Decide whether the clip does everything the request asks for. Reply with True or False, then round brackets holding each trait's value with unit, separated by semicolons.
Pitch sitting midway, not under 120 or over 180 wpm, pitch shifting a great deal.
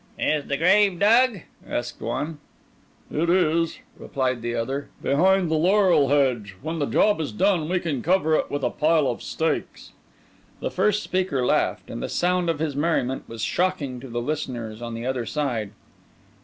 True (150 Hz; 175 wpm; 5.8 semitones)